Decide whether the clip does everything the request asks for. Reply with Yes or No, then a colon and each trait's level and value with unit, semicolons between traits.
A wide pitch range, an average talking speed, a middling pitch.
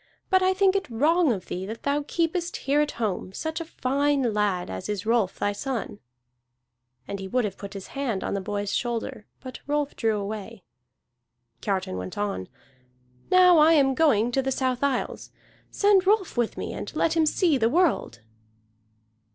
No: wide, 7.3 semitones; average, 180 wpm; very high, 255 Hz